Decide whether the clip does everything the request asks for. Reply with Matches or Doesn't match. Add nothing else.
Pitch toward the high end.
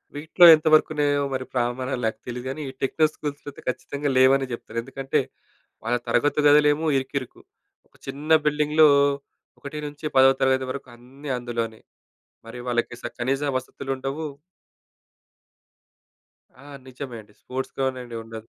Doesn't match